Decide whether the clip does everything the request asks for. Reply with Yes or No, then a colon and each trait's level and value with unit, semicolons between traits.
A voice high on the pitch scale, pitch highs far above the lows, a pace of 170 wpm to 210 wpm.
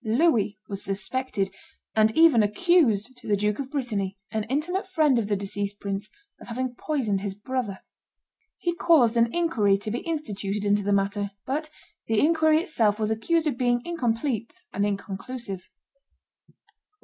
No: high, 225 Hz; wide, 6.0 semitones; average, 155 wpm